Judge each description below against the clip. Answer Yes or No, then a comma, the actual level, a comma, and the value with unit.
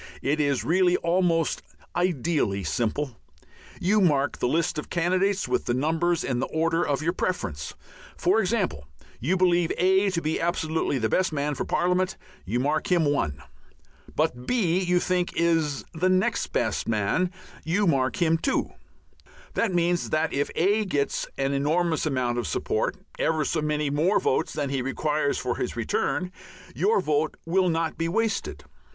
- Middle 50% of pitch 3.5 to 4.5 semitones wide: Yes, average, 4.1 semitones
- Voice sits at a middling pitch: Yes, medium, 165 Hz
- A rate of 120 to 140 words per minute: No, average, 160 wpm